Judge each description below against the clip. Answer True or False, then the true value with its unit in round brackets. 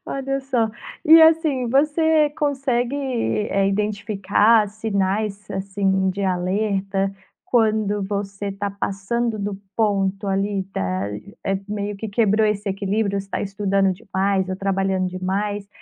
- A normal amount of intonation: False (2.0 semitones)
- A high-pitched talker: True (200 Hz)